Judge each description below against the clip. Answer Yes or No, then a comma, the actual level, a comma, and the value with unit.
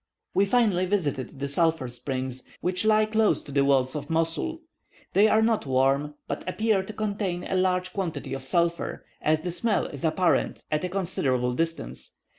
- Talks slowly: No, average, 175 wpm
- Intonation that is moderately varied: No, wide, 6.1 semitones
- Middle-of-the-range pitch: Yes, medium, 170 Hz